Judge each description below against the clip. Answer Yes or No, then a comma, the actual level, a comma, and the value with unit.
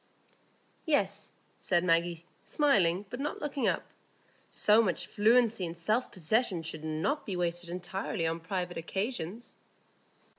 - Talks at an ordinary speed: No, slow, 125 wpm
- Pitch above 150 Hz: Yes, medium, 185 Hz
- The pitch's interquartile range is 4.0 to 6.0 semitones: Yes, average, 5.1 semitones